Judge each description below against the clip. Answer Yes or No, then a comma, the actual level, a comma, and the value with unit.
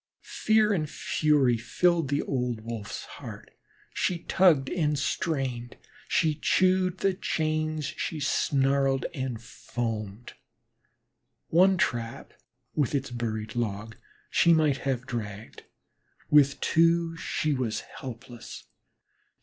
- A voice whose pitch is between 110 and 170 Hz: Yes, medium, 140 Hz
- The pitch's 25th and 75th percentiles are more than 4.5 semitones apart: Yes, average, 5.3 semitones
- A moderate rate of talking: No, slow, 110 wpm